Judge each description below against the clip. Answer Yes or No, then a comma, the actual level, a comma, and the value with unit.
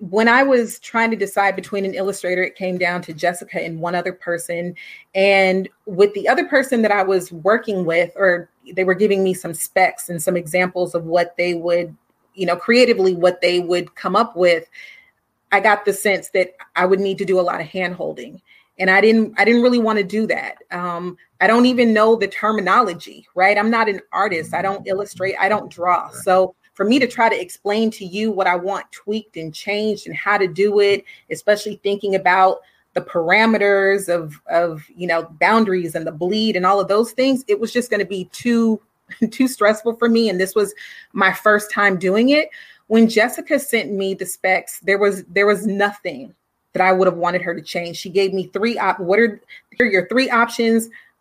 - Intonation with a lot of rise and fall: No, average, 3.3 semitones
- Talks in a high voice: Yes, high, 195 Hz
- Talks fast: Yes, fast, 215 wpm